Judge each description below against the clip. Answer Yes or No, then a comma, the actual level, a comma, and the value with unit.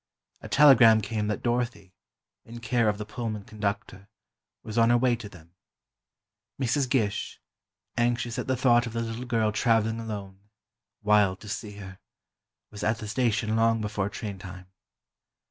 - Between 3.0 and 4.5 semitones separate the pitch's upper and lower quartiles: No, narrow, 2.4 semitones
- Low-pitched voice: Yes, low, 110 Hz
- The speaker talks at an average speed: Yes, average, 160 wpm